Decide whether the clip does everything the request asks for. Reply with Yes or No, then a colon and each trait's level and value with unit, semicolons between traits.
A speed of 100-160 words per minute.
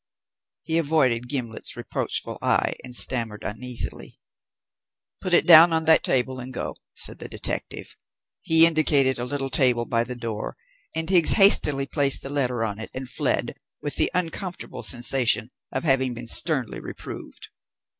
Yes: average, 155 wpm